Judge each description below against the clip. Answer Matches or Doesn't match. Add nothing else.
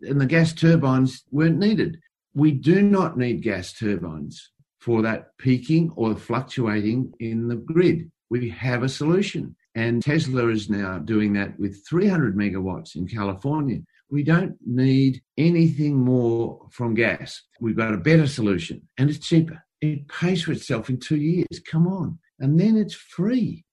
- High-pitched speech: Doesn't match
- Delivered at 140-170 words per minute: Matches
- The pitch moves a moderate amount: Doesn't match